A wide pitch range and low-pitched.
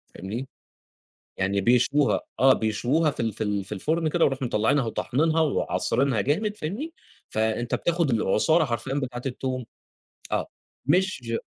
Yes: wide, 5.8 semitones; low, 130 Hz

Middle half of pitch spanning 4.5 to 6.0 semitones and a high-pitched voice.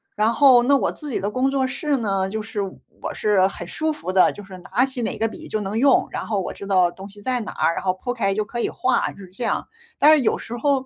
Yes: average, 4.9 semitones; high, 220 Hz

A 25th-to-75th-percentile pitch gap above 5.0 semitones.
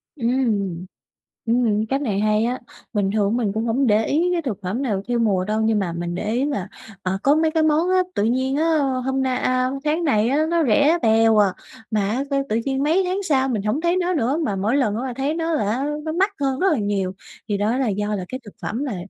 Yes: wide, 5.5 semitones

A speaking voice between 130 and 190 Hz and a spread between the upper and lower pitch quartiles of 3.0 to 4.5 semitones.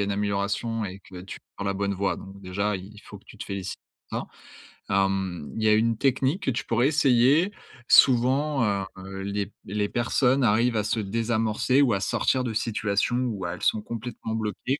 No: low, 105 Hz; average, 3.4 semitones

